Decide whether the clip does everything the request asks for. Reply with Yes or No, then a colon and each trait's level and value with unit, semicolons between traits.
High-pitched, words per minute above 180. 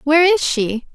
Yes: very high, 295 Hz; average, 190 wpm